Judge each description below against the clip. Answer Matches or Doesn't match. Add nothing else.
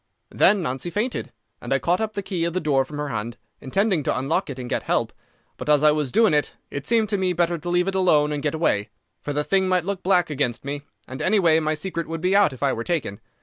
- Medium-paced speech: Doesn't match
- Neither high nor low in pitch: Matches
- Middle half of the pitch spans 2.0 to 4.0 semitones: Doesn't match